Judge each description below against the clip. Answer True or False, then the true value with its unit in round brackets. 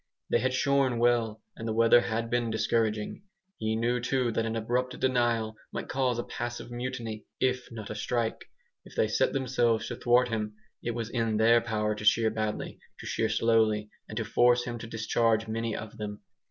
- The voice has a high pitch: False (115 Hz)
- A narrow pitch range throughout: True (1.7 semitones)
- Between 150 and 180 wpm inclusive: False (195 wpm)